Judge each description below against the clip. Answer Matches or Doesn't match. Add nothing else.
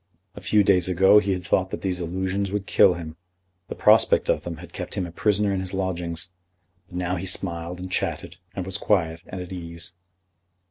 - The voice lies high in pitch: Doesn't match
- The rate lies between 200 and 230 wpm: Matches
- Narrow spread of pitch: Matches